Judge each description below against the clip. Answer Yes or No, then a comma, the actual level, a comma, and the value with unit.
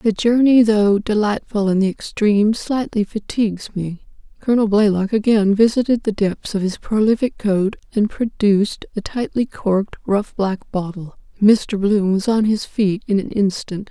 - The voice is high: Yes, high, 210 Hz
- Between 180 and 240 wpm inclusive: No, average, 160 wpm